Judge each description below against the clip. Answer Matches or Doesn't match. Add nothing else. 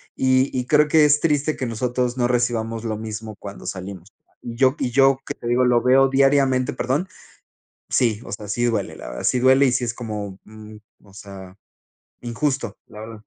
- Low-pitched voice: Matches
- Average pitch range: Matches